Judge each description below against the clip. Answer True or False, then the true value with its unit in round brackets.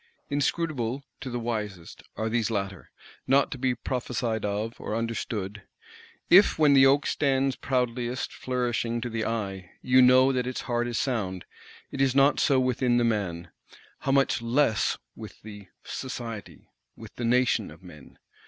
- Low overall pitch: True (120 Hz)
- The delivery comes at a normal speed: True (160 wpm)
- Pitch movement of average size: True (3.0 semitones)